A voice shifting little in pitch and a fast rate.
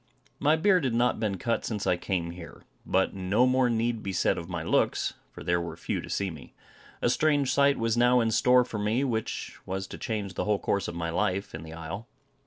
No: average, 5.2 semitones; fast, 230 wpm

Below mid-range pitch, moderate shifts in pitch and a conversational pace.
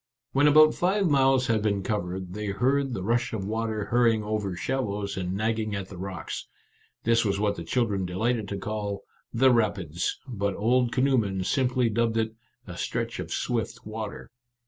Yes: low, 110 Hz; average, 3.5 semitones; average, 185 wpm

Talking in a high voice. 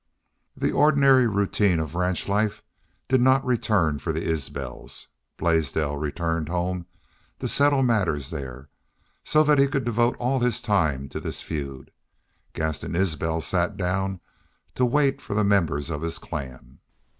No: very low, 90 Hz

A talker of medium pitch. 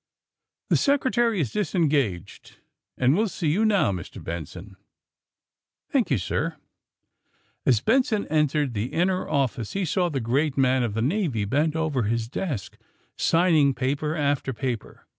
Yes: medium, 145 Hz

